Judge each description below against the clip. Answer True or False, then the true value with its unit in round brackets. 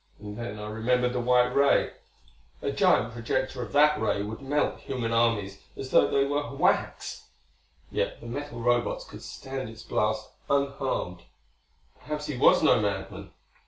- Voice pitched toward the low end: True (120 Hz)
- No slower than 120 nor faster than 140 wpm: False (160 wpm)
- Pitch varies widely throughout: False (4.3 semitones)